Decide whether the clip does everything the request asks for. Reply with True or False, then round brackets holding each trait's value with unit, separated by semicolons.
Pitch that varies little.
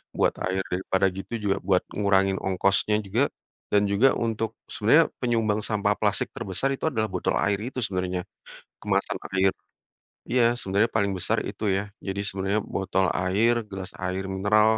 True (2.1 semitones)